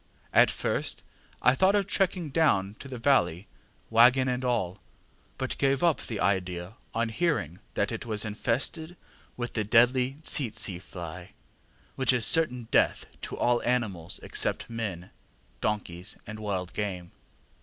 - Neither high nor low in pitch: No, low, 115 Hz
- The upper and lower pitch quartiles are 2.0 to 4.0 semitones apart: No, wide, 5.4 semitones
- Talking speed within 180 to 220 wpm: No, average, 145 wpm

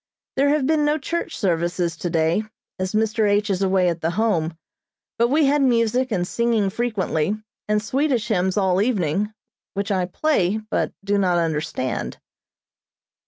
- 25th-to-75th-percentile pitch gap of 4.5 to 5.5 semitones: Yes, average, 4.8 semitones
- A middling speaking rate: Yes, average, 155 wpm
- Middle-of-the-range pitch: No, high, 205 Hz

